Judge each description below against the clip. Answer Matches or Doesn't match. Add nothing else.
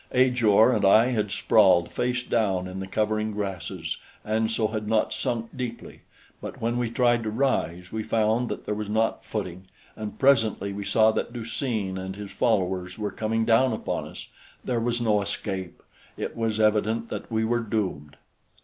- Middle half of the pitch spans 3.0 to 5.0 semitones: Doesn't match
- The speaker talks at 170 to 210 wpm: Matches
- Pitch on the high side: Doesn't match